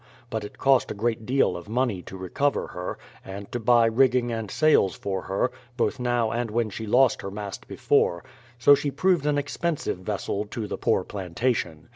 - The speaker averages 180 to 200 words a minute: Yes, average, 190 wpm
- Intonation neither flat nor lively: Yes, average, 4.6 semitones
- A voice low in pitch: Yes, low, 115 Hz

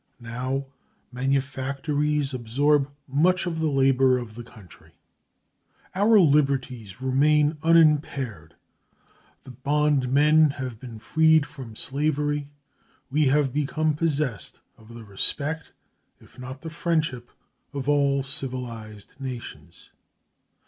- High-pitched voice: No, medium, 140 Hz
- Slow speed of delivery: Yes, slow, 105 wpm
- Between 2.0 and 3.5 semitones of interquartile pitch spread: Yes, average, 3.0 semitones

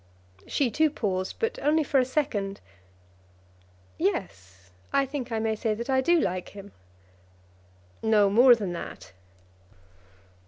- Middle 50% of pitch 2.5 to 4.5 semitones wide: No, wide, 5.5 semitones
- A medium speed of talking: No, slow, 130 wpm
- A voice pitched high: Yes, high, 220 Hz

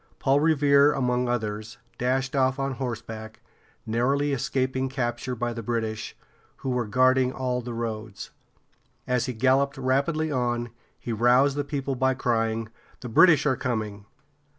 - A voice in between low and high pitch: No, low, 125 Hz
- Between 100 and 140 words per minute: No, average, 150 wpm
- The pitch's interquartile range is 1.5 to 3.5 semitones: Yes, narrow, 2.6 semitones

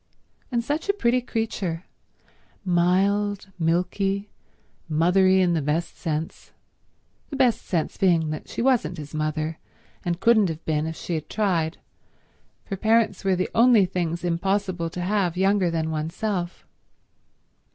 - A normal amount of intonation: Yes, average, 3.8 semitones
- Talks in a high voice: No, medium, 180 Hz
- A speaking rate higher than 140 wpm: No, slow, 135 wpm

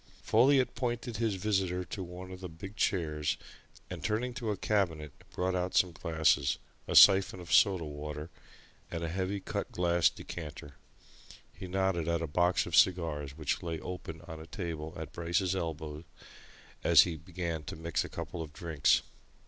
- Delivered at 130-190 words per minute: Yes, average, 170 wpm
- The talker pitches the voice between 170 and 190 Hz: No, very low, 85 Hz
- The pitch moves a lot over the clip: No, average, 2.9 semitones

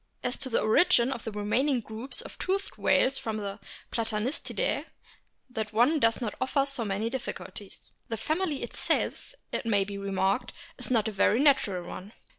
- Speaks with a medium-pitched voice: No, high, 230 Hz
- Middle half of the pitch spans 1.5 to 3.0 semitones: No, average, 4.3 semitones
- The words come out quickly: No, average, 170 wpm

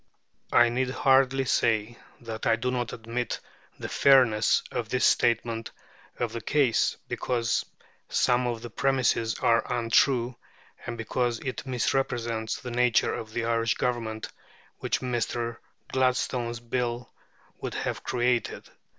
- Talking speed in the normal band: No, slow, 130 wpm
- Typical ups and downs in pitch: No, narrow, 1.6 semitones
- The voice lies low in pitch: Yes, low, 120 Hz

